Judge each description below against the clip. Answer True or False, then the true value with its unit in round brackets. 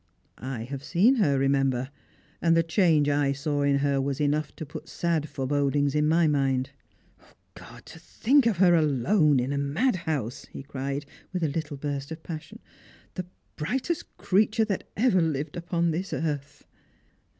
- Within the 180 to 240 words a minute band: False (165 wpm)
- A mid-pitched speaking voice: True (150 Hz)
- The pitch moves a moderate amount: True (3.5 semitones)